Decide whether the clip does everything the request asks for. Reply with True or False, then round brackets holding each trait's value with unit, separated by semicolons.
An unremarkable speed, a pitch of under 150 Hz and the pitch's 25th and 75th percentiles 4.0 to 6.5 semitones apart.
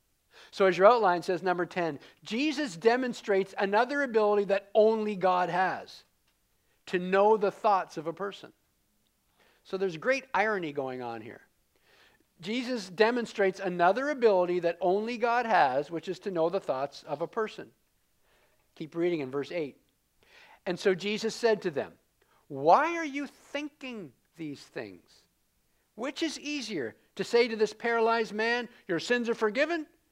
False (150 wpm; 205 Hz; 4.8 semitones)